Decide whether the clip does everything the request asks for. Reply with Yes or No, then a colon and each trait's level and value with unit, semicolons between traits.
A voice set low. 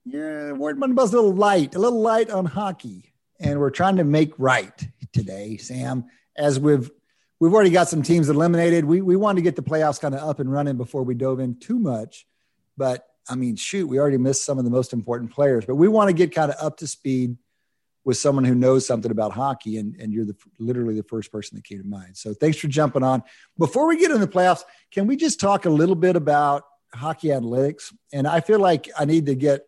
No: medium, 145 Hz